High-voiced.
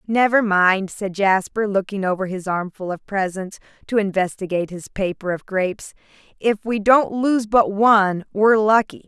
Yes: high, 200 Hz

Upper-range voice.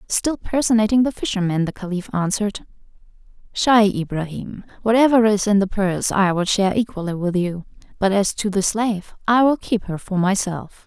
Yes: high, 205 Hz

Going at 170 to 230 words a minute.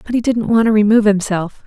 No: fast, 250 wpm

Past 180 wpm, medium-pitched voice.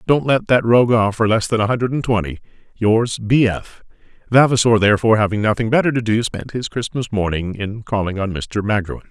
No: average, 200 wpm; low, 110 Hz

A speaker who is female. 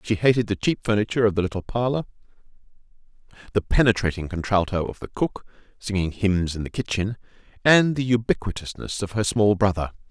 No: male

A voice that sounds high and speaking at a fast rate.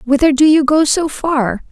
Yes: very high, 290 Hz; fast, 210 wpm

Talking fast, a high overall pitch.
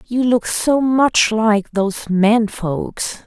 No: average, 145 wpm; high, 220 Hz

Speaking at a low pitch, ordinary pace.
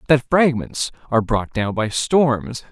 Yes: low, 125 Hz; average, 155 wpm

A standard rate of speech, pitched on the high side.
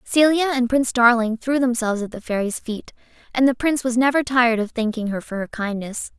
No: fast, 215 wpm; high, 240 Hz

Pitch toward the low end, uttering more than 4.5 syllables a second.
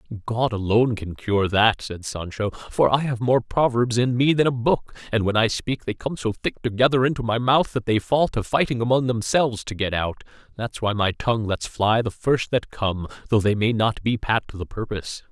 Yes: low, 115 Hz; 5.3 syllables/s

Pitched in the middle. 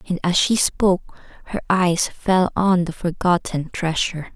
Yes: medium, 180 Hz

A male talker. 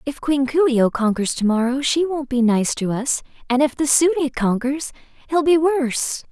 No: female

